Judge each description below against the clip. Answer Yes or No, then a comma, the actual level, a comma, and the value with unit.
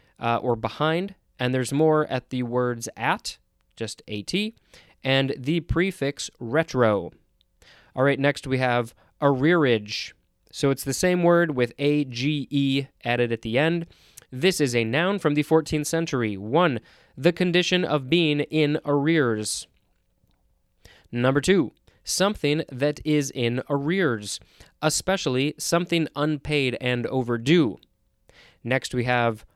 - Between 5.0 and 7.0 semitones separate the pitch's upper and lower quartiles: No, average, 4.6 semitones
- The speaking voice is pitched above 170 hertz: No, medium, 140 Hz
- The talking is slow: Yes, slow, 130 wpm